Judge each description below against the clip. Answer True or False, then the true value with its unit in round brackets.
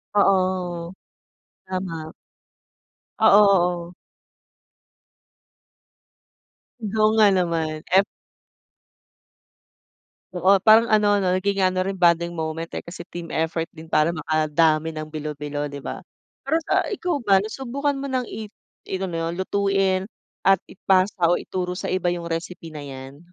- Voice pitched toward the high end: False (180 Hz)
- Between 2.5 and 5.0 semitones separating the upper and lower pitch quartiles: True (3.3 semitones)